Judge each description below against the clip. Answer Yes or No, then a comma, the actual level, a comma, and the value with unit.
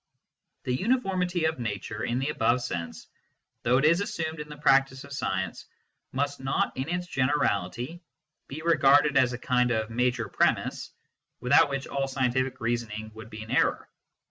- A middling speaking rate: Yes, average, 170 wpm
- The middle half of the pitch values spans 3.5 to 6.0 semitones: Yes, average, 4.0 semitones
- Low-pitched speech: Yes, low, 130 Hz